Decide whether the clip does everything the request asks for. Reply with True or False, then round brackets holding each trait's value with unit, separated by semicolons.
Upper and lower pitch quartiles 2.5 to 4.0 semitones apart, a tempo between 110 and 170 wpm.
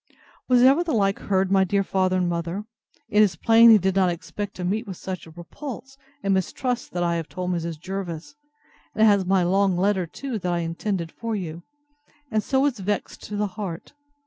False (3.4 semitones; 205 wpm)